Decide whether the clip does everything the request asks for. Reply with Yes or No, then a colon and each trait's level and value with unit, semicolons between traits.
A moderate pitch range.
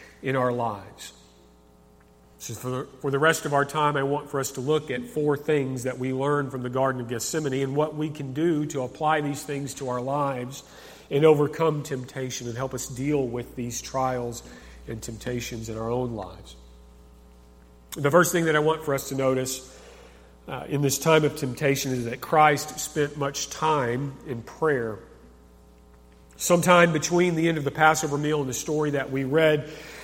Yes: average, 4.0 semitones